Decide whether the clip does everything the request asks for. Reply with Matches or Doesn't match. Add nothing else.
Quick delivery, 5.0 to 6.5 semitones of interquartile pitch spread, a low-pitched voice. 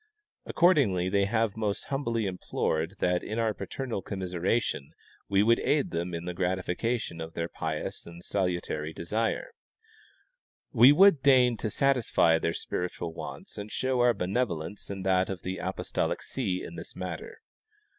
Doesn't match